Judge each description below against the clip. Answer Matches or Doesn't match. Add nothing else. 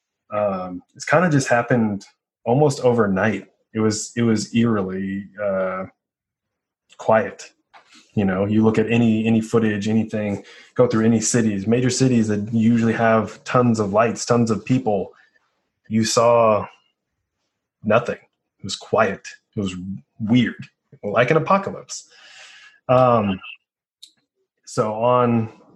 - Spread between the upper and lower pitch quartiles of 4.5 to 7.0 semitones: Doesn't match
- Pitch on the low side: Matches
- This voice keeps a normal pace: Doesn't match